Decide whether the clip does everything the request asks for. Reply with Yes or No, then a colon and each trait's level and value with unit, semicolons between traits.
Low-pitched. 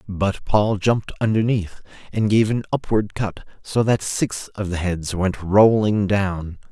Yes: low, 100 Hz